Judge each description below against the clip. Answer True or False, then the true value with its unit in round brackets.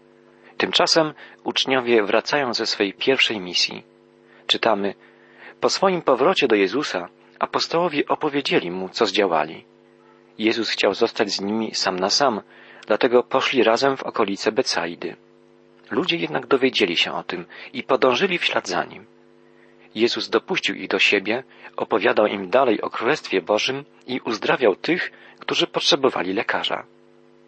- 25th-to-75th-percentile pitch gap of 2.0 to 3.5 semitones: False (5.3 semitones)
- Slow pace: False (135 wpm)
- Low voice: True (115 Hz)